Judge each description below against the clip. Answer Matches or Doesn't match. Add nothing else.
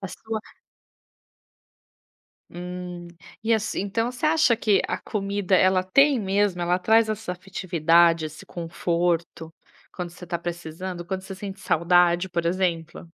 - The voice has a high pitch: Doesn't match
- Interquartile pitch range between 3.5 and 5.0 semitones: Doesn't match